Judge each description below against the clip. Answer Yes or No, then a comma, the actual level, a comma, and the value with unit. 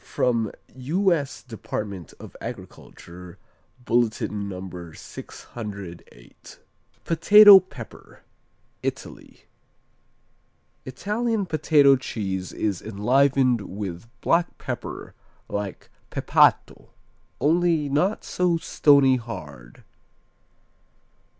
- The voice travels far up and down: Yes, wide, 8.2 semitones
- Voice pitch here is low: Yes, low, 120 Hz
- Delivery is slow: Yes, slow, 75 wpm